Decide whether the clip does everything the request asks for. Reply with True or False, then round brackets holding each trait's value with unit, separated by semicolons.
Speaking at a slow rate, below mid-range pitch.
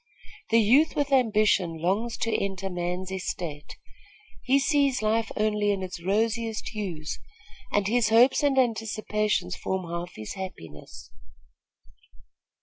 False (125 wpm; 210 Hz)